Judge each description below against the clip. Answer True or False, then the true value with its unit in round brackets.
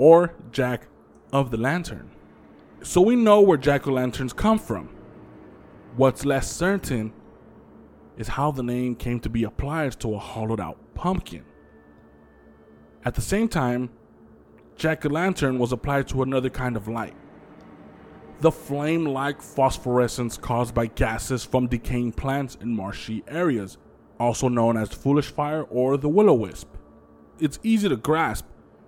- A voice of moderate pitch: False (120 Hz)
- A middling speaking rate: True (150 wpm)